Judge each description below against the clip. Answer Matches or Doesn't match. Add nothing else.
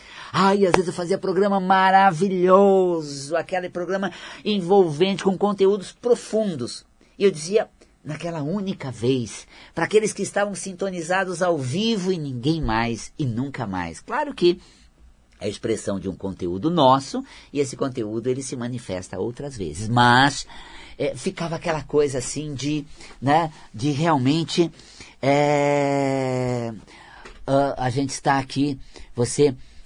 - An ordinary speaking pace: Matches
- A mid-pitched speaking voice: Matches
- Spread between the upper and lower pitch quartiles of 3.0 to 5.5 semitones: Doesn't match